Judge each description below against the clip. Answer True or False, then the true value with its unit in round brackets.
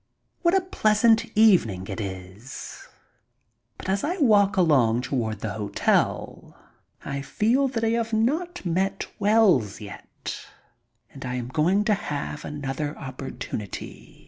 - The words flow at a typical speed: False (130 wpm)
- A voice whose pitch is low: False (165 Hz)